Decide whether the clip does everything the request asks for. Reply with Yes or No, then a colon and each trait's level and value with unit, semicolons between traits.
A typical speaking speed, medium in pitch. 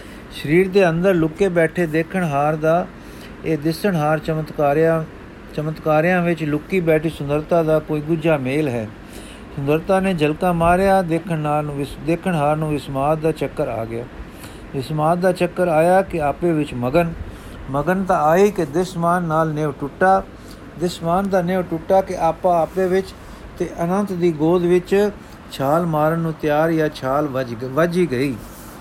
Yes: average, 155 wpm; medium, 160 Hz